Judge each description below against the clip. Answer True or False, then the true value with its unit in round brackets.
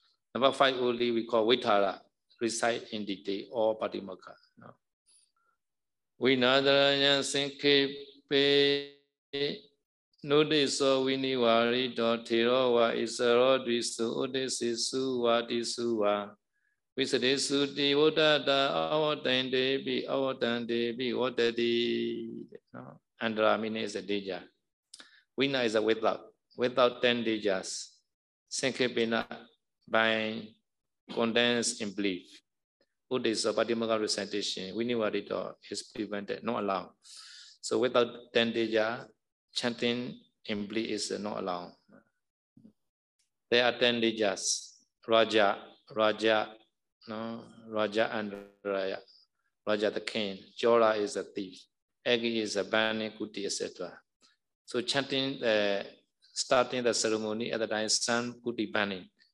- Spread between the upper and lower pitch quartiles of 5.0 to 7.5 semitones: False (3.2 semitones)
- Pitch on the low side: True (120 Hz)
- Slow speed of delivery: True (120 wpm)